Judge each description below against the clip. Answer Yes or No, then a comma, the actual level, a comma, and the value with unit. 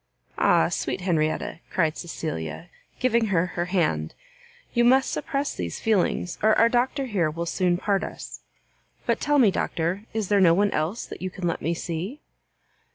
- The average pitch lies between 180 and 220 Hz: Yes, medium, 185 Hz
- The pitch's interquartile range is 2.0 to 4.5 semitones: No, average, 5.0 semitones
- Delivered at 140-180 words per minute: Yes, average, 170 wpm